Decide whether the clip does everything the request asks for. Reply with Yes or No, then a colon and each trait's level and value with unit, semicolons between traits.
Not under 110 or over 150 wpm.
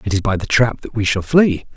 No: fast, 305 wpm